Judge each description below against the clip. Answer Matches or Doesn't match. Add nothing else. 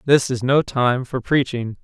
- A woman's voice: Doesn't match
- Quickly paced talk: Doesn't match